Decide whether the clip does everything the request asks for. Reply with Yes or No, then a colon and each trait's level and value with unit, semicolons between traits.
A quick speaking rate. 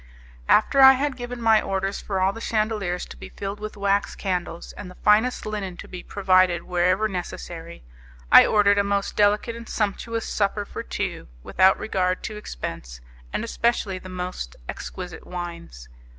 No: average, 165 wpm